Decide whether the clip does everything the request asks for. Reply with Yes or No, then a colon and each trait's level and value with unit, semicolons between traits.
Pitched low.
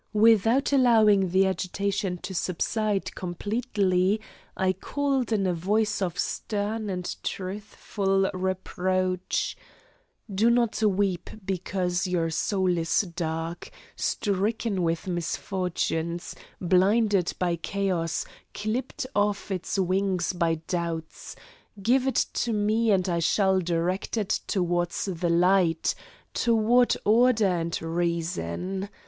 No: high, 190 Hz